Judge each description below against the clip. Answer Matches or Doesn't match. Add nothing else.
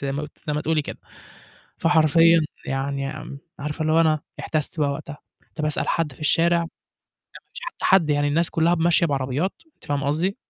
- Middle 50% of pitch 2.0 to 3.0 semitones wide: Matches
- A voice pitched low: Doesn't match